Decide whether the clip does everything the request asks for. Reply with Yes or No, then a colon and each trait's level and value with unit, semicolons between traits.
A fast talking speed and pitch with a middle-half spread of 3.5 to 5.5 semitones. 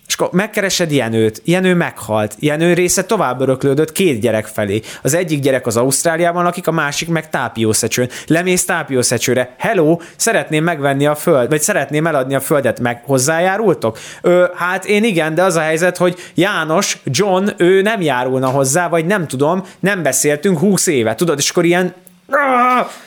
Yes: fast, 165 wpm; average, 5.2 semitones